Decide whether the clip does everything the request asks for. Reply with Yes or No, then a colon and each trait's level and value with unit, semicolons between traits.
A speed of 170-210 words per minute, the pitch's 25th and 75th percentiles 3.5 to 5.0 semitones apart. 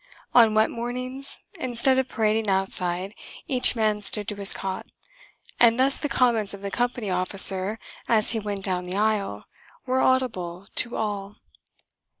No: average, 150 wpm; average, 3.8 semitones